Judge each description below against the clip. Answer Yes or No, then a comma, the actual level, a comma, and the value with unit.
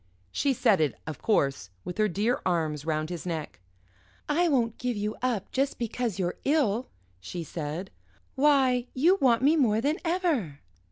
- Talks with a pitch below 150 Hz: No, high, 225 Hz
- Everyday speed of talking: Yes, average, 165 wpm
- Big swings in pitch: Yes, wide, 7.9 semitones